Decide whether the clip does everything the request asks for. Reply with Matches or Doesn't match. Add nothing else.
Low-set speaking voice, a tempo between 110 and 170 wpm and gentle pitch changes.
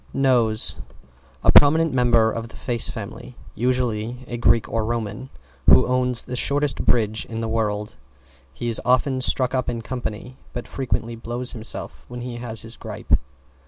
Matches